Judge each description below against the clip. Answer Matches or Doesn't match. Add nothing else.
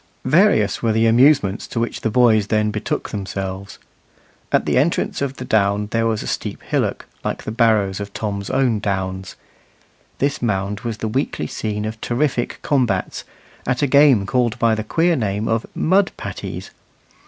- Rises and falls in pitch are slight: Doesn't match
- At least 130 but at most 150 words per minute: Doesn't match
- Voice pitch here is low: Matches